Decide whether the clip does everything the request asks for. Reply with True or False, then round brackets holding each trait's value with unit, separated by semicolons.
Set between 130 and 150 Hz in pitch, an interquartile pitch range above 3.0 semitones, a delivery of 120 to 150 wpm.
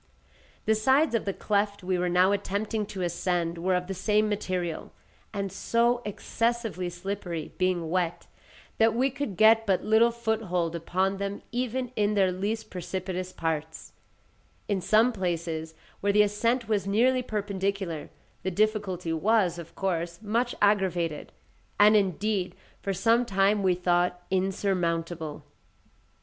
False (195 Hz; 3.4 semitones; 140 wpm)